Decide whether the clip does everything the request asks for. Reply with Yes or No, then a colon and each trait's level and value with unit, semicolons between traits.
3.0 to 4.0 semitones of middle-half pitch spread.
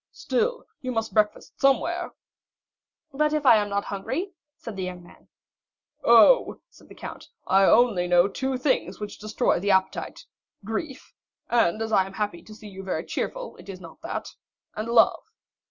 No: average, 5.0 semitones